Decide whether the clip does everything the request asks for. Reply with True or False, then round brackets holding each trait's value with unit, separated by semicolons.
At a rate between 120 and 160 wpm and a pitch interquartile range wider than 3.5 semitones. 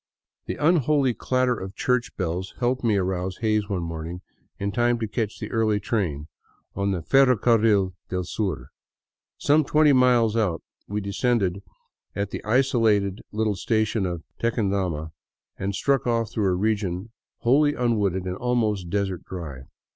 True (150 wpm; 4.2 semitones)